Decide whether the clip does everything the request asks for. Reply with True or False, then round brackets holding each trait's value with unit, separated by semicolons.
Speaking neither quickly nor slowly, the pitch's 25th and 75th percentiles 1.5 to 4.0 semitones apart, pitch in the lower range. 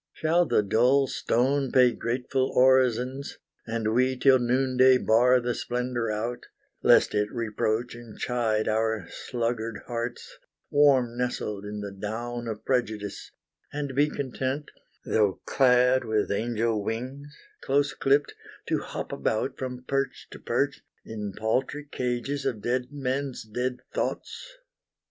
False (130 wpm; 2.8 semitones; 125 Hz)